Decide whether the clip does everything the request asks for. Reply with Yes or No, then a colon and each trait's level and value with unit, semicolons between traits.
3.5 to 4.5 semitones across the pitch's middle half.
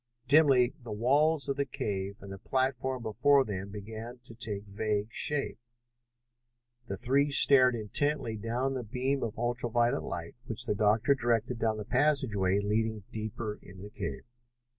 Yes: average, 4.0 semitones